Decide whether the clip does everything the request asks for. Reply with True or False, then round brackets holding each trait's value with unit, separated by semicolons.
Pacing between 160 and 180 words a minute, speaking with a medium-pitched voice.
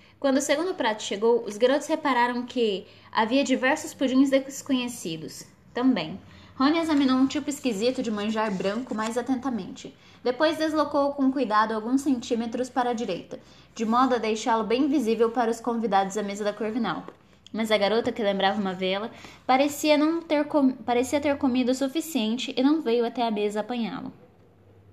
False (165 wpm; 245 Hz)